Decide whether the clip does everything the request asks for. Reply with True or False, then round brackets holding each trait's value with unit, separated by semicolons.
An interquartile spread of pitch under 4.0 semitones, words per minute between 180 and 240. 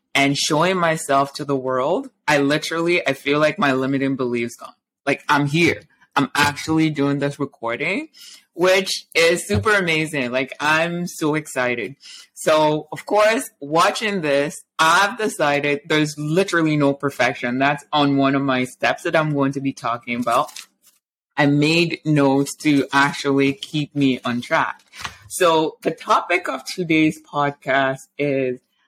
False (2.8 semitones; 150 wpm)